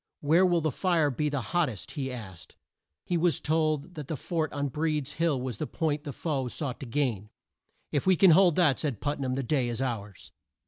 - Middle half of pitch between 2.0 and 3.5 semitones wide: No, average, 4.0 semitones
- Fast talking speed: Yes, fast, 220 wpm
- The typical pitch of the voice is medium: Yes, medium, 145 Hz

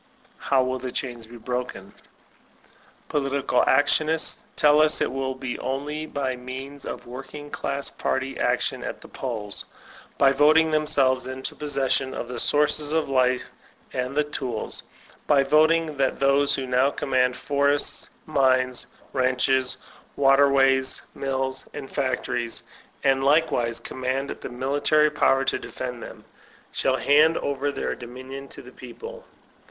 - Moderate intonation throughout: No, narrow, 2.0 semitones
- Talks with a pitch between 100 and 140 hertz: Yes, low, 135 Hz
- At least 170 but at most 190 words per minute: No, average, 140 wpm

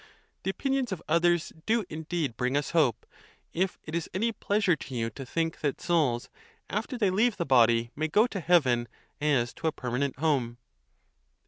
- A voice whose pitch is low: No, medium, 160 Hz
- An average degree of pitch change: No, wide, 6.6 semitones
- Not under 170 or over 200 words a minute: Yes, average, 180 wpm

